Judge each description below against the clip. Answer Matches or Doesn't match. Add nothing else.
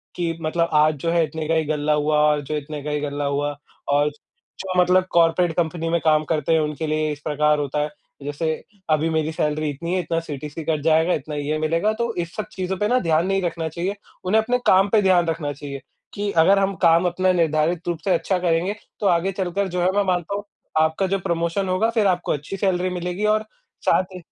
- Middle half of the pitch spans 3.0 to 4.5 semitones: Matches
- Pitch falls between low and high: Matches